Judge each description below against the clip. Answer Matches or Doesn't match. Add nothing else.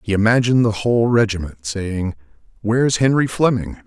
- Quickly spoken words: Doesn't match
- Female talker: Doesn't match